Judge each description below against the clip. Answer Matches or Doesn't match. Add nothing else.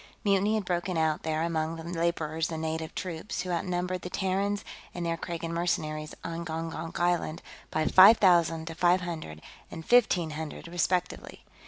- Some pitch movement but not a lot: Doesn't match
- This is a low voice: Doesn't match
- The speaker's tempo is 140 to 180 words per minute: Matches